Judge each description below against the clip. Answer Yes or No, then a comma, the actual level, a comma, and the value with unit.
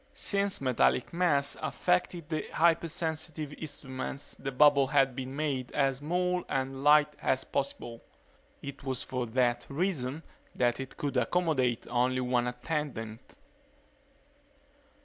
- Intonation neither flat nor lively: Yes, average, 3.3 semitones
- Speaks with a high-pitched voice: No, medium, 140 Hz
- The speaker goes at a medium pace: No, slow, 120 wpm